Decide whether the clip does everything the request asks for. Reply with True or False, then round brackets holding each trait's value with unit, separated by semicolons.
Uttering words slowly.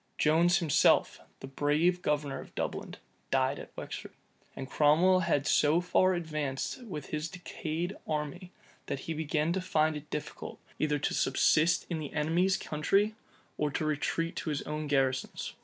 False (155 wpm)